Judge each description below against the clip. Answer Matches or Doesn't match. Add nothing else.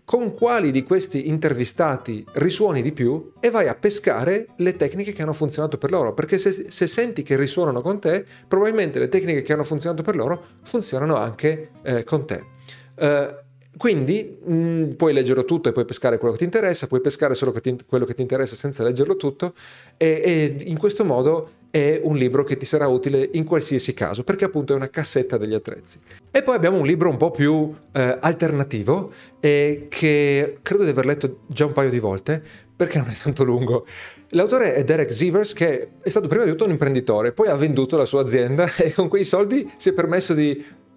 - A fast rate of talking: Matches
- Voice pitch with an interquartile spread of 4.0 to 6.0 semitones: Matches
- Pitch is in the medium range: Matches